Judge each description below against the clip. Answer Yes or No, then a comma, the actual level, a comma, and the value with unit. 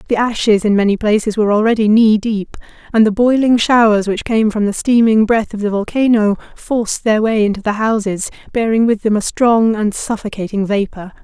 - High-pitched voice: Yes, high, 215 Hz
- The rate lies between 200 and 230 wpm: No, average, 190 wpm